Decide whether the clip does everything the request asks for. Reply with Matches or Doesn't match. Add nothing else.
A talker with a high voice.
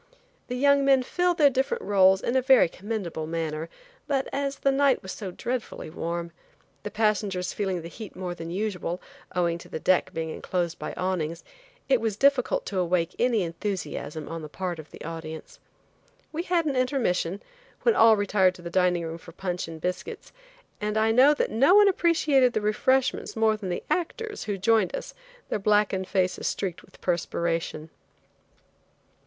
Matches